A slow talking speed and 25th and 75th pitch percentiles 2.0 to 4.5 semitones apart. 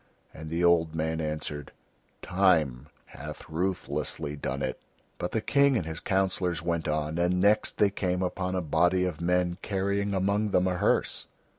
No: average, 165 wpm; average, 3.0 semitones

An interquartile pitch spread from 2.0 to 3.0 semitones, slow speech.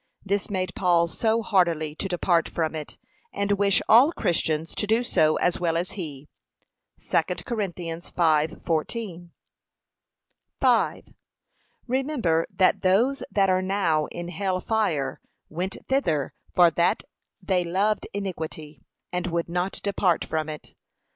No: average, 3.5 semitones; slow, 130 wpm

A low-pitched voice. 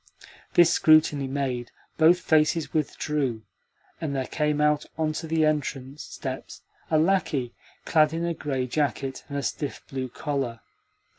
No: medium, 150 Hz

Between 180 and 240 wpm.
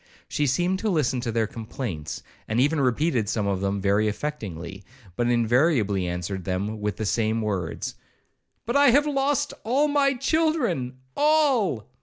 No: average, 150 wpm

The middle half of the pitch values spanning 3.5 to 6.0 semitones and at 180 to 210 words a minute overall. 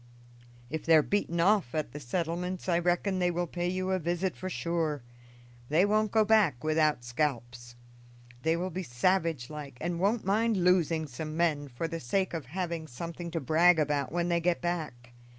No: average, 3.1 semitones; average, 185 wpm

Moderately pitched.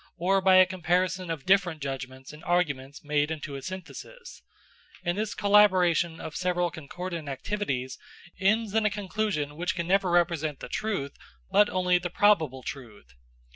Yes: medium, 175 Hz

